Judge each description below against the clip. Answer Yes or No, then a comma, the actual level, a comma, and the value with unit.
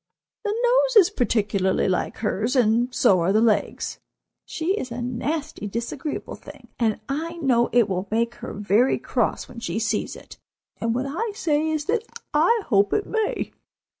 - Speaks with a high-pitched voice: Yes, high, 245 Hz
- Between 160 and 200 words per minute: Yes, average, 170 wpm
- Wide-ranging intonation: Yes, wide, 6.9 semitones